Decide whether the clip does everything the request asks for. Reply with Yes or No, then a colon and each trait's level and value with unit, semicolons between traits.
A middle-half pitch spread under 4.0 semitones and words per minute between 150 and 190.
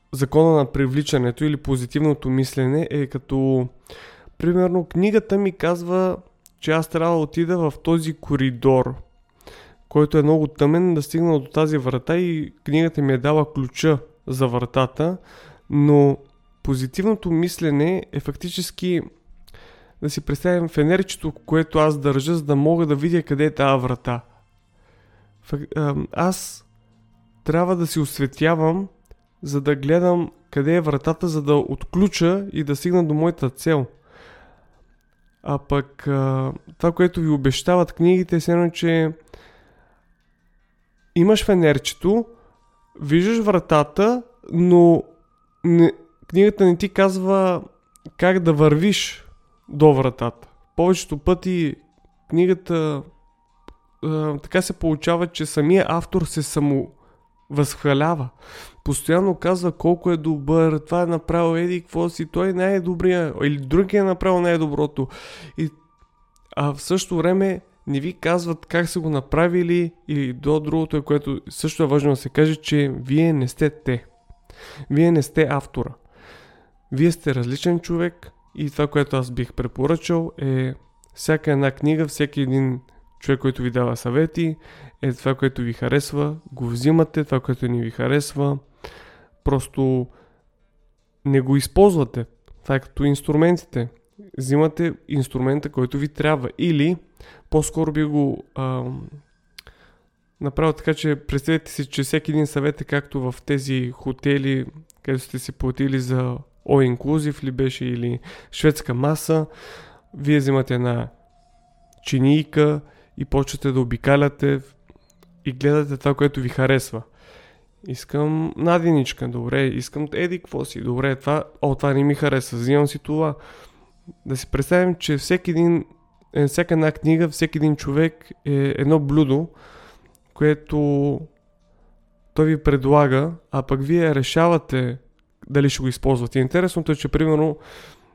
No: average, 3.6 semitones; average, 130 wpm